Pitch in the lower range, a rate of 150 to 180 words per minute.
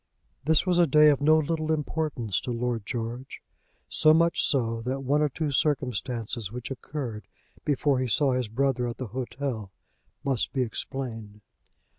Yes: low, 130 Hz; average, 160 wpm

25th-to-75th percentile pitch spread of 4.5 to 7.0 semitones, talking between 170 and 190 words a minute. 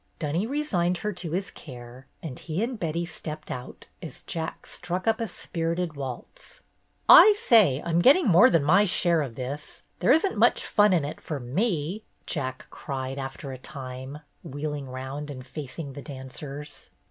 Yes: average, 5.1 semitones; average, 175 wpm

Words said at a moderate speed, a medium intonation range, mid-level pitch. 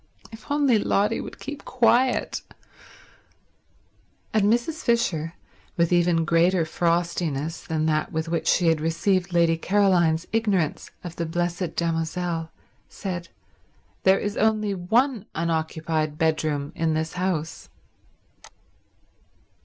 No: slow, 115 wpm; average, 3.8 semitones; medium, 170 Hz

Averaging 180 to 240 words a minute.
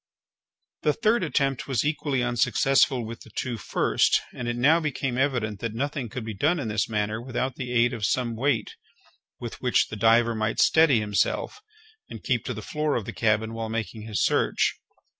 Yes: average, 190 wpm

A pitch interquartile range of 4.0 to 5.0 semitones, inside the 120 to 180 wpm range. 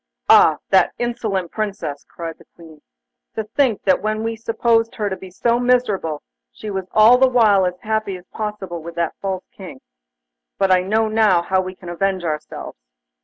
No: average, 3.6 semitones; average, 175 wpm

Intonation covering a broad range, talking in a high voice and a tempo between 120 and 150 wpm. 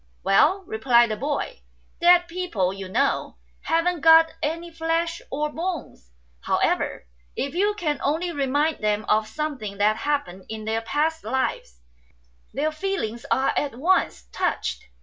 Yes: wide, 7.2 semitones; very high, 290 Hz; average, 140 wpm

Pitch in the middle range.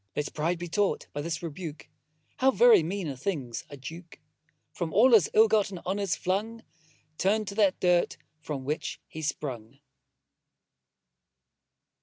Yes: medium, 175 Hz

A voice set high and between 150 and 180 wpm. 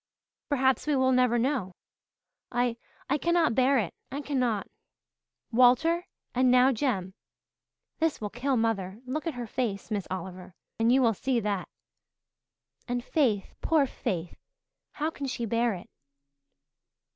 No: high, 245 Hz; average, 140 wpm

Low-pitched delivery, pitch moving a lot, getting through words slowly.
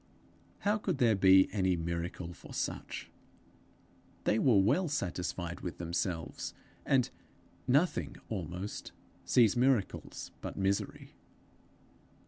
Yes: very low, 95 Hz; wide, 6.1 semitones; slow, 105 wpm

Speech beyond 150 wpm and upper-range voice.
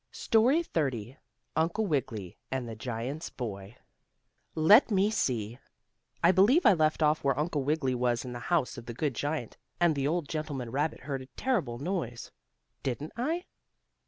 No: average, 160 wpm; medium, 145 Hz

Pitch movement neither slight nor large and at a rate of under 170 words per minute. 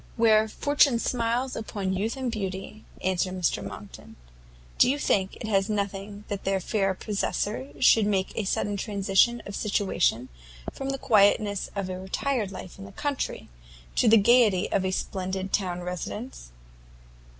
Yes: average, 3.0 semitones; average, 150 wpm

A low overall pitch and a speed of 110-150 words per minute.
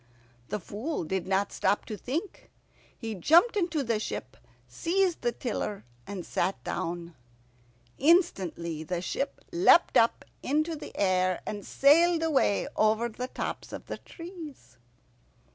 No: high, 230 Hz; slow, 135 wpm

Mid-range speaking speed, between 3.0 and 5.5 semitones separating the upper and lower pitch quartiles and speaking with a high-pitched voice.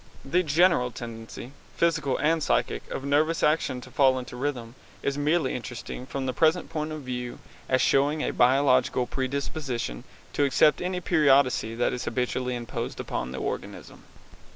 No: average, 155 wpm; average, 3.5 semitones; low, 135 Hz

